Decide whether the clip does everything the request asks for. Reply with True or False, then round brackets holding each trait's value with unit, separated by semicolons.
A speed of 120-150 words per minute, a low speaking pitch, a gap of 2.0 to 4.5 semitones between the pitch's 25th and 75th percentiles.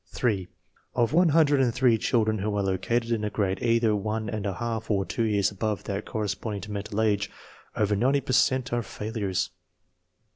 False (195 wpm; 110 Hz; 2.7 semitones)